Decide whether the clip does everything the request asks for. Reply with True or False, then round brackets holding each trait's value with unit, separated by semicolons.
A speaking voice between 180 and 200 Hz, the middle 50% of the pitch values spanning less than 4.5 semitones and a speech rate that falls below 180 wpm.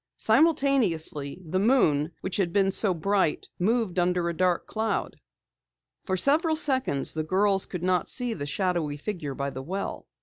False (185 Hz; 5.2 semitones; 160 wpm)